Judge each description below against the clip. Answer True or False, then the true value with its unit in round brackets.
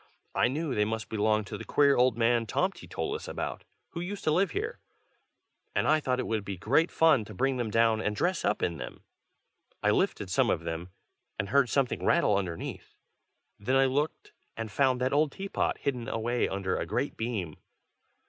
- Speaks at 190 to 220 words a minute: True (195 wpm)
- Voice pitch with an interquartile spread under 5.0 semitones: False (5.3 semitones)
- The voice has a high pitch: False (125 Hz)